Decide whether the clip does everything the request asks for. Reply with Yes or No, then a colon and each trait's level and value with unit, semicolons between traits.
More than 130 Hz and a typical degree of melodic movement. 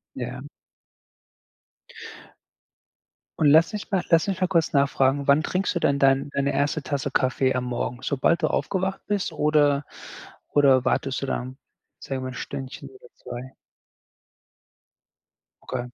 Yes: medium, 140 Hz; average, 3.2 semitones